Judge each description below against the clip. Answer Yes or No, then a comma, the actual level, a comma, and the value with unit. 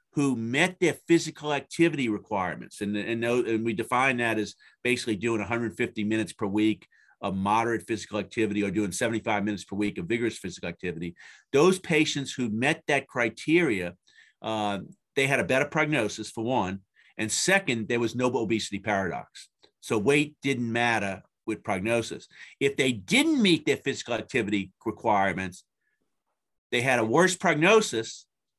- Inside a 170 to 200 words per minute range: No, average, 155 wpm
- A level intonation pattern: No, average, 4.8 semitones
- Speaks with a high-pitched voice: No, low, 115 Hz